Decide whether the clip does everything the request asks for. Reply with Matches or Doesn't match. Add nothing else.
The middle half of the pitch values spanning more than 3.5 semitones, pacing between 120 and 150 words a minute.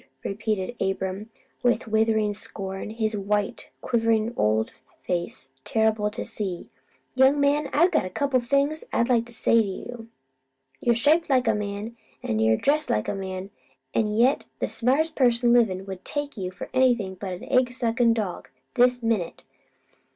Doesn't match